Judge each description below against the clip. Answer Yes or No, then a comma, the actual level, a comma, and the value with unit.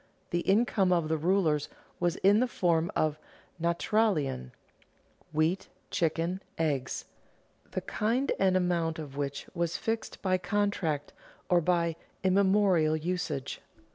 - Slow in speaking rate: Yes, slow, 120 wpm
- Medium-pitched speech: Yes, medium, 175 Hz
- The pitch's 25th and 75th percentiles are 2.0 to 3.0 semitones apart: No, average, 3.5 semitones